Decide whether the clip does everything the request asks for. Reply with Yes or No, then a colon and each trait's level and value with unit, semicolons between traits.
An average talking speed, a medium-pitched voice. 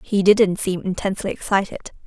No: average, 145 wpm; high, 195 Hz